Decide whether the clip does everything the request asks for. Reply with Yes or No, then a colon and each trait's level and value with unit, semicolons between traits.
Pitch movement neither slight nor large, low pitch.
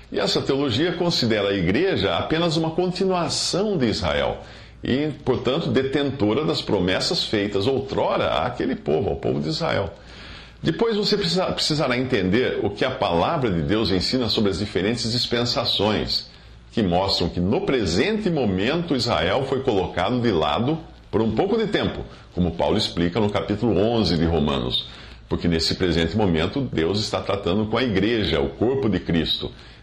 No: wide, 7.2 semitones; low, 110 Hz